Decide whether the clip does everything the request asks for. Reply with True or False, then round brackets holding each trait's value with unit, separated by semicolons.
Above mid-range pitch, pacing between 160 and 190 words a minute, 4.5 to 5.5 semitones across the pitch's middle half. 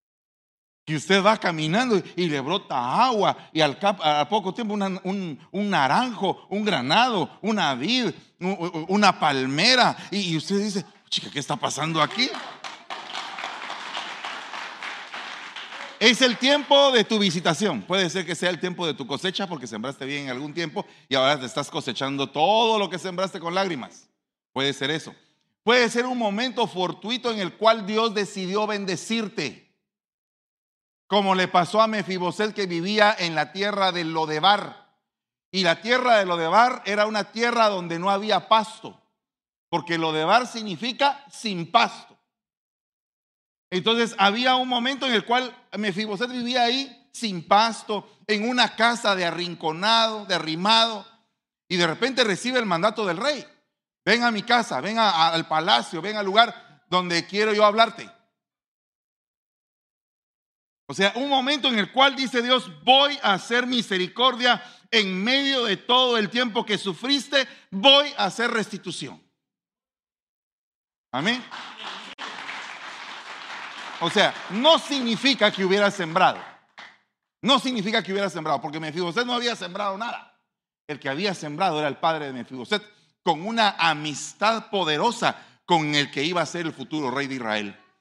False (200 Hz; 150 wpm; 5.1 semitones)